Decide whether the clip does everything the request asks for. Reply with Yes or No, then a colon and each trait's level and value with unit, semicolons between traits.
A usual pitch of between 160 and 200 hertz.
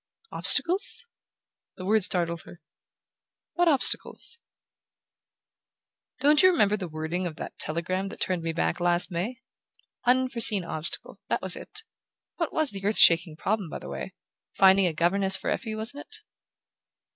Yes: high, 190 Hz